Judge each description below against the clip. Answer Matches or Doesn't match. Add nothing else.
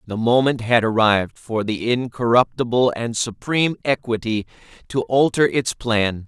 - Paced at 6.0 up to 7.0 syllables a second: Doesn't match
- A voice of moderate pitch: Doesn't match